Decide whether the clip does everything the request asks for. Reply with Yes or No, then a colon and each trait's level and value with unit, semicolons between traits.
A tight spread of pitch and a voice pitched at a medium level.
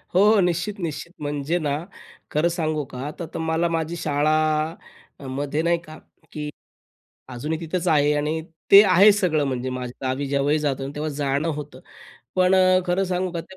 No: average, 3.4 semitones; medium, 155 Hz